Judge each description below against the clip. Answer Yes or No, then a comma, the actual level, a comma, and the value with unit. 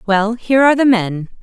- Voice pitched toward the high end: Yes, high, 220 Hz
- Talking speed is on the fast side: Yes, fast, 210 wpm